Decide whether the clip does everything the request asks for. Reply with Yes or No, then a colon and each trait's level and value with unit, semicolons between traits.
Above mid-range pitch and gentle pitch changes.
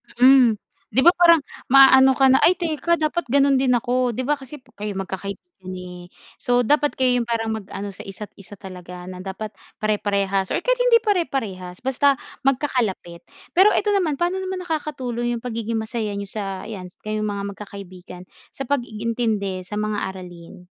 No: high, 230 Hz; wide, 5.5 semitones